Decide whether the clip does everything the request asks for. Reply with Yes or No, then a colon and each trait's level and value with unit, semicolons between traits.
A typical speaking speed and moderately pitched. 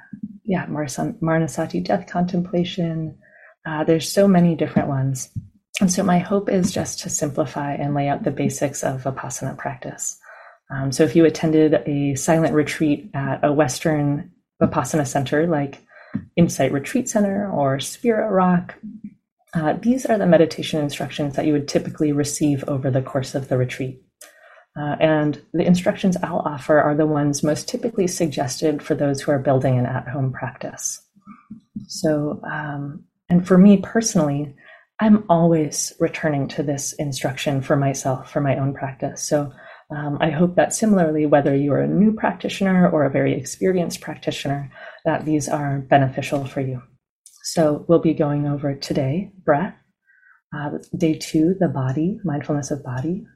Yes: average, 155 wpm; medium, 155 Hz